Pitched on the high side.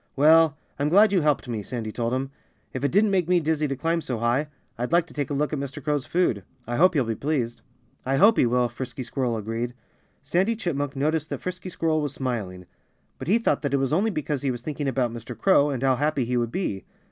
No: medium, 140 Hz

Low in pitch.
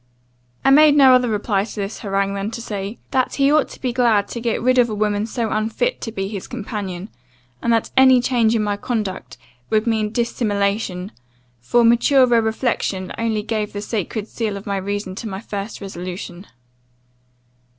No: high, 215 Hz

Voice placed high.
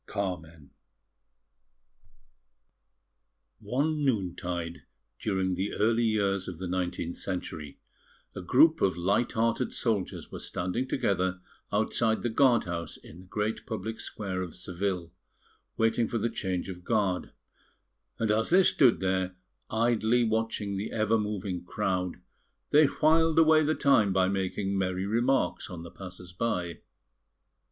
No: low, 100 Hz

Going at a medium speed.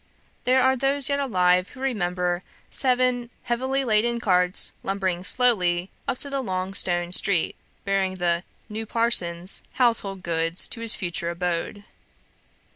No: slow, 130 wpm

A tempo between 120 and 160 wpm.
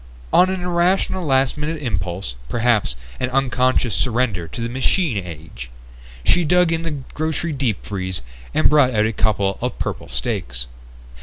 Yes: average, 155 wpm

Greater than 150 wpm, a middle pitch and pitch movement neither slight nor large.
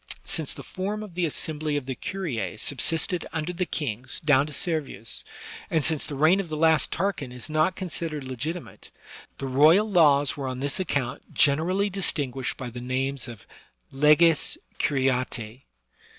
Yes: average, 160 wpm; medium, 150 Hz; average, 4.3 semitones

